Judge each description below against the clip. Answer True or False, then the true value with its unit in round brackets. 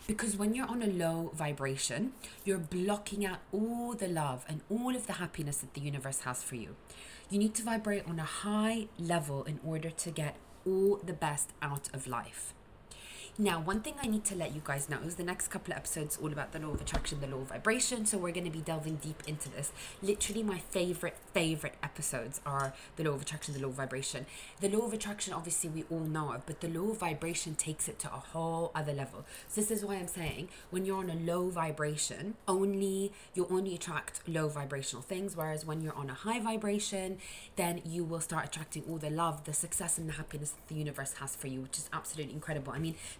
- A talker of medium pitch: True (165 Hz)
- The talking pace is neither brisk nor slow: False (225 wpm)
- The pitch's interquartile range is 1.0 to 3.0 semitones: False (4.5 semitones)